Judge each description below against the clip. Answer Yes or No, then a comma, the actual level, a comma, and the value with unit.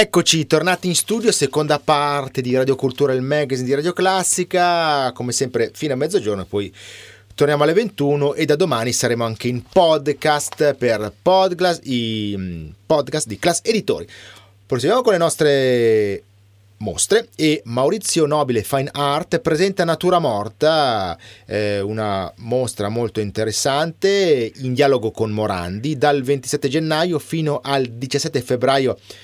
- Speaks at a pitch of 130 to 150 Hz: Yes, medium, 140 Hz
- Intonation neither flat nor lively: No, wide, 5.8 semitones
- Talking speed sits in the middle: Yes, average, 130 wpm